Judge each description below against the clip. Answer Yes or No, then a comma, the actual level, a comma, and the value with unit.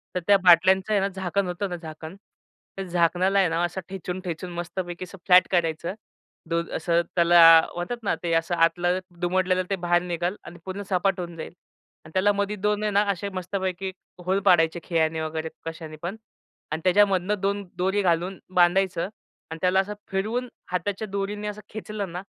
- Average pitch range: No, narrow, 2.3 semitones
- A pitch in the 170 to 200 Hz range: Yes, medium, 185 Hz